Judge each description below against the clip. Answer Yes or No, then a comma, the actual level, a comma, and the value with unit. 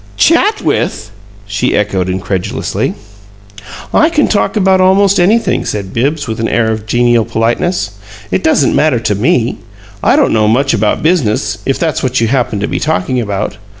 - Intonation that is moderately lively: No, wide, 8.4 semitones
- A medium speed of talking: Yes, average, 170 wpm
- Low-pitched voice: Yes, low, 120 Hz